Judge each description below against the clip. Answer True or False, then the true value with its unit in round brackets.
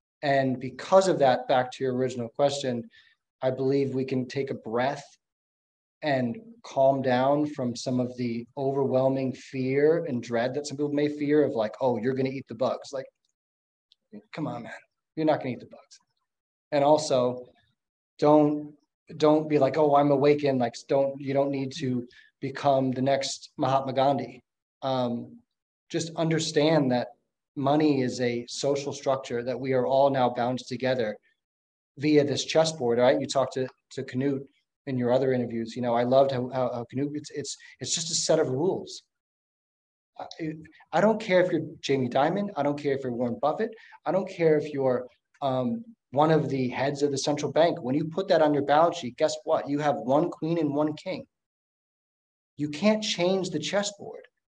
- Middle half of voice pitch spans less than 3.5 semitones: True (3.1 semitones)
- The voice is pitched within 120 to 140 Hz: True (135 Hz)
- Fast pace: False (185 wpm)